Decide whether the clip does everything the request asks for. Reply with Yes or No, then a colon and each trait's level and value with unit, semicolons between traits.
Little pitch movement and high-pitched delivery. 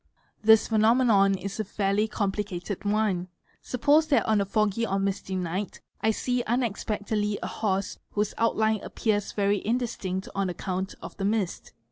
Yes: narrow, 2.2 semitones; high, 205 Hz